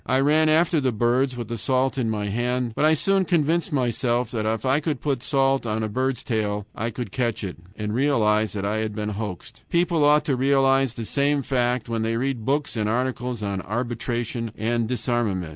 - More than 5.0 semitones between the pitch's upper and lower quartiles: No, average, 3.6 semitones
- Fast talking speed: Yes, fast, 210 wpm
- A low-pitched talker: Yes, low, 120 Hz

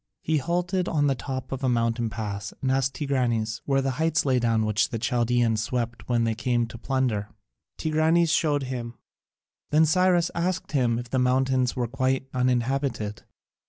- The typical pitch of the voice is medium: No, low, 130 Hz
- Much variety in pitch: No, average, 3.6 semitones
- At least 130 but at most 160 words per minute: No, average, 170 wpm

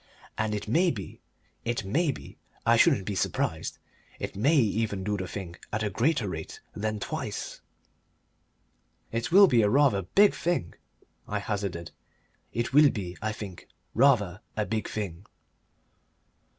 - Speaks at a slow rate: No, average, 150 wpm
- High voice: No, low, 105 Hz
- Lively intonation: No, average, 4.3 semitones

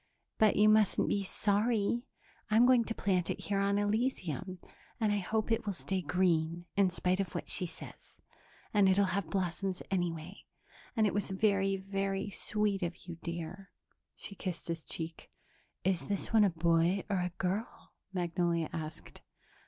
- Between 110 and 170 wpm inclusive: Yes, average, 165 wpm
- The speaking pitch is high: Yes, high, 195 Hz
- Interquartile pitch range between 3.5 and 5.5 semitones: No, average, 2.8 semitones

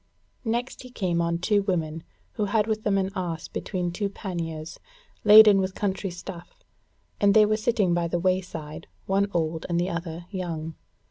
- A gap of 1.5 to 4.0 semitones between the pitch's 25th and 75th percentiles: Yes, average, 3.5 semitones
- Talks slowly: No, average, 175 wpm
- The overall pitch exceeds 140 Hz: Yes, medium, 185 Hz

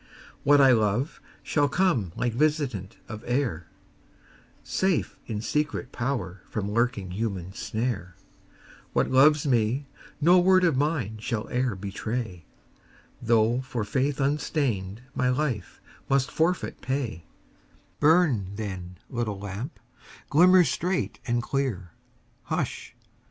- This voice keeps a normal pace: No, slow, 115 wpm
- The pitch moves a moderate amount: No, wide, 5.7 semitones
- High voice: No, low, 125 Hz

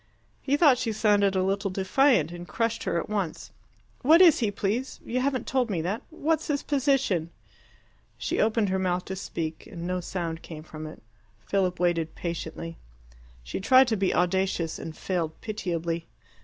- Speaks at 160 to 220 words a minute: Yes, average, 170 wpm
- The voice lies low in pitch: No, high, 190 Hz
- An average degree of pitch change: No, wide, 5.7 semitones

